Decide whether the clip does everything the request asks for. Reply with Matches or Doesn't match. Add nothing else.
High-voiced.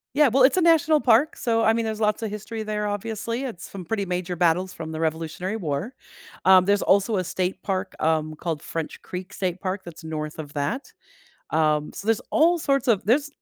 Matches